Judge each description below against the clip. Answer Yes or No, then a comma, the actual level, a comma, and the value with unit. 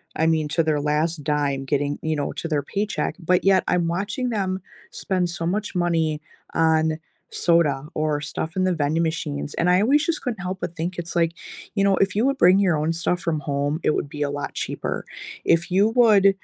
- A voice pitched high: No, medium, 165 Hz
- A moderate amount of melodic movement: Yes, average, 3.7 semitones